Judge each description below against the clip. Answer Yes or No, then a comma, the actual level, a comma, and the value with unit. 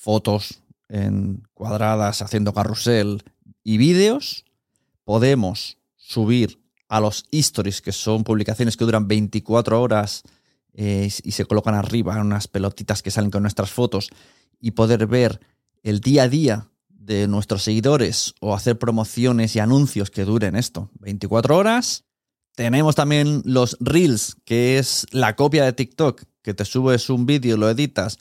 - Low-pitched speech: Yes, low, 110 Hz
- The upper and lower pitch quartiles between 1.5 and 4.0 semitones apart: Yes, average, 3.3 semitones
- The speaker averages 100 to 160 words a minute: Yes, average, 145 wpm